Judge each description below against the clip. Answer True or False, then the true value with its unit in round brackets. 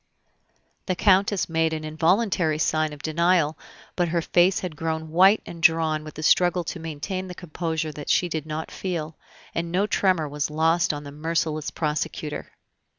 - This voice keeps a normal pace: True (170 wpm)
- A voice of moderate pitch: True (160 Hz)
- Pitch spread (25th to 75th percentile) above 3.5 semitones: False (2.4 semitones)